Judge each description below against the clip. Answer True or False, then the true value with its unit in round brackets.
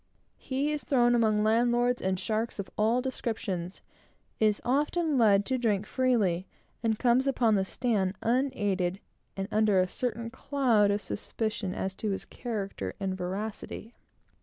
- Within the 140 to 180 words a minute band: True (145 wpm)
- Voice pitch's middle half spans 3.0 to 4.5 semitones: True (3.9 semitones)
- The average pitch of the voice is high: True (220 Hz)